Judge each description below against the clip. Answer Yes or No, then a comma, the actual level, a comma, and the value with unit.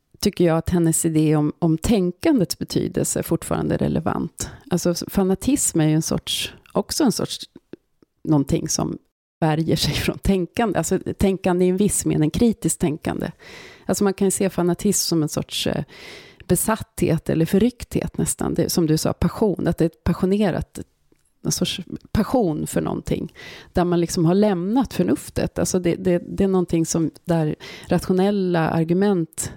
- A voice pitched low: No, medium, 175 Hz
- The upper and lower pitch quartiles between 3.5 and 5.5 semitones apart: No, average, 3.1 semitones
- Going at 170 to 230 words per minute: No, average, 160 wpm